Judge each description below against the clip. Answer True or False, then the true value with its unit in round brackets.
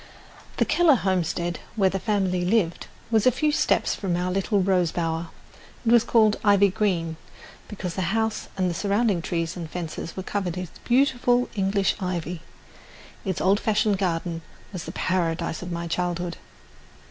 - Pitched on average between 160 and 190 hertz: True (185 Hz)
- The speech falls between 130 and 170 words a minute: True (160 wpm)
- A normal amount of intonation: True (3.3 semitones)